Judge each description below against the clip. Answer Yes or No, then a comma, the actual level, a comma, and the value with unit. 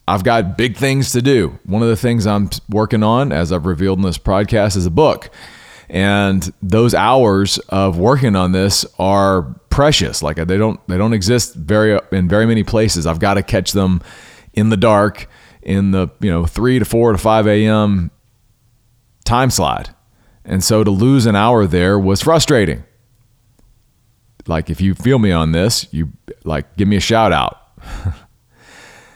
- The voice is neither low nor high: No, low, 105 Hz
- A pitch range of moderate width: Yes, average, 3.5 semitones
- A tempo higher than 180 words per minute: No, average, 175 wpm